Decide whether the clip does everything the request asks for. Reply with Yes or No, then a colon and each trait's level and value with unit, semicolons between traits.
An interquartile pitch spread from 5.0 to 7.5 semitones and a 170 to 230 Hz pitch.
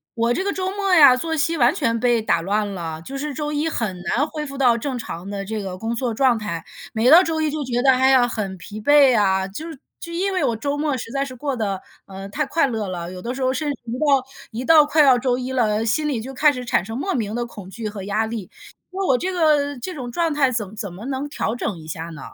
No: wide, 5.4 semitones; very high, 250 Hz